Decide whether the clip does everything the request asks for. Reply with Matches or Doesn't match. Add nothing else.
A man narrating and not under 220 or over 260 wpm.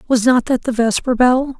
Doesn't match